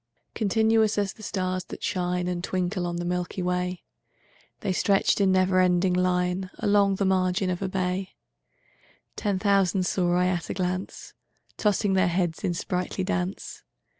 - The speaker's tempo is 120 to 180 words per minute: Yes, average, 160 wpm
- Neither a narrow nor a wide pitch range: No, narrow, 1.5 semitones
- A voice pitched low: No, medium, 185 Hz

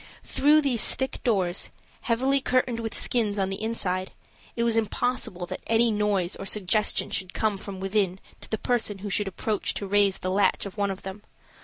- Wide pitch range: No, average, 3.1 semitones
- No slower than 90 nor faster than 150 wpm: No, average, 190 wpm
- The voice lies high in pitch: Yes, high, 205 Hz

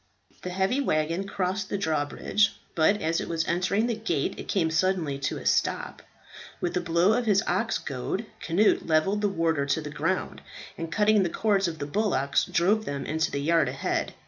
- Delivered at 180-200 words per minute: Yes, average, 195 wpm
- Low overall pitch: No, medium, 175 Hz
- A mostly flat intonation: No, average, 4.3 semitones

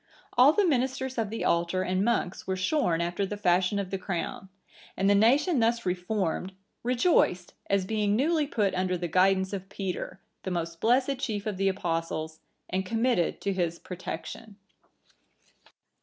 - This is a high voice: Yes, high, 195 Hz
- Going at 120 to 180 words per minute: Yes, average, 165 wpm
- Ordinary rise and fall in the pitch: Yes, average, 4.2 semitones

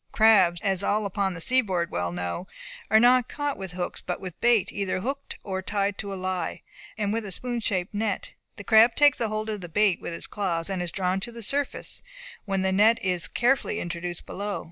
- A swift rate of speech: Yes, fast, 210 wpm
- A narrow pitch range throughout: No, average, 3.4 semitones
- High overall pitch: Yes, high, 200 Hz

